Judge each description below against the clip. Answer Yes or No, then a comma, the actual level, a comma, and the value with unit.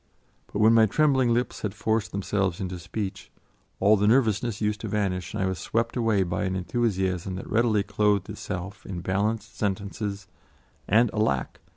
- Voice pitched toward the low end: Yes, low, 105 Hz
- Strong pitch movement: No, average, 2.7 semitones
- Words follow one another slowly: No, average, 170 wpm